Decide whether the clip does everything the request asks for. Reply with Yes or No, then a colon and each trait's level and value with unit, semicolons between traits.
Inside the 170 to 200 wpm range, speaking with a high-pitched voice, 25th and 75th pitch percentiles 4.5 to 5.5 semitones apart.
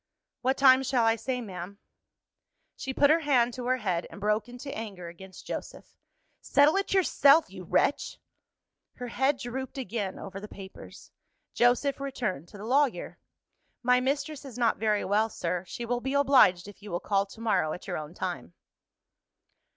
Yes: average, 175 wpm; high, 235 Hz; average, 5.2 semitones